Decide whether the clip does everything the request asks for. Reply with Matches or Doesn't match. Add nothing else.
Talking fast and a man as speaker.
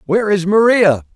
Doesn't match